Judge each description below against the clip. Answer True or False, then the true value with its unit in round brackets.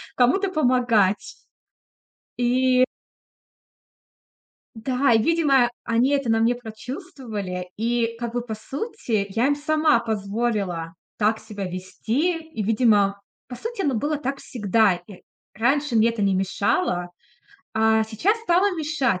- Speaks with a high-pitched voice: True (235 Hz)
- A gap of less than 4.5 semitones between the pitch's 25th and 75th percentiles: False (4.8 semitones)